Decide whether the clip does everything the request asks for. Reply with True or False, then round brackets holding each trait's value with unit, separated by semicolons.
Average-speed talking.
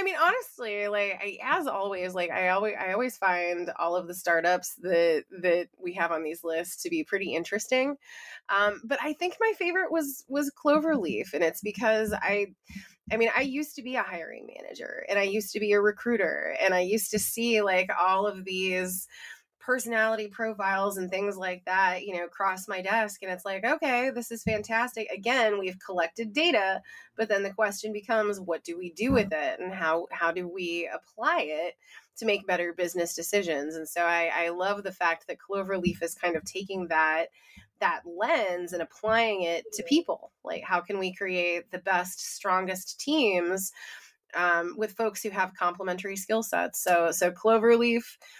True (190 wpm)